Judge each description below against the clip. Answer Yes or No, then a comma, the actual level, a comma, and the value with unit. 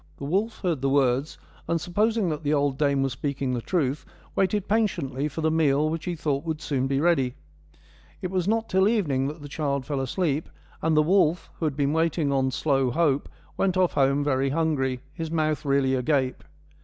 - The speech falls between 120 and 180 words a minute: No, average, 200 wpm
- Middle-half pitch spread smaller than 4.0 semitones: Yes, average, 3.6 semitones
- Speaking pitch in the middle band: Yes, medium, 150 Hz